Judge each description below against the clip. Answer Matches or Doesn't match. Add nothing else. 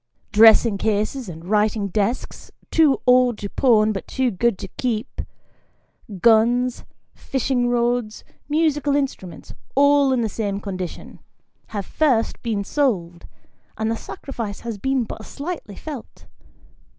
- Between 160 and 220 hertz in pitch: Doesn't match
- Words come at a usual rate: Doesn't match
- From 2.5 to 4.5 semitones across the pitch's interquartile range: Matches